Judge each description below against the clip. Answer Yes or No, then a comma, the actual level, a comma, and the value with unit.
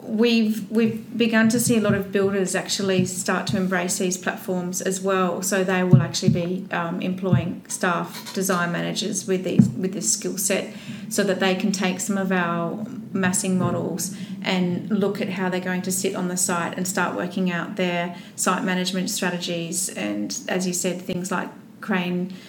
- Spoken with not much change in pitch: Yes, narrow, 1.9 semitones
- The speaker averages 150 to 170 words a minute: No, average, 185 wpm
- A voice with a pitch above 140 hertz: Yes, high, 190 Hz